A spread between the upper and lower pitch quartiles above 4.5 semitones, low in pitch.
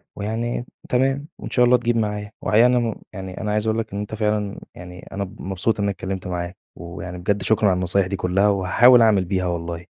No: average, 3.3 semitones; low, 100 Hz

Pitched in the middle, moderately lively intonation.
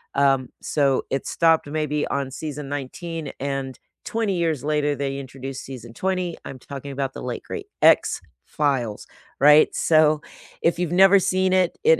Yes: medium, 150 Hz; average, 3.8 semitones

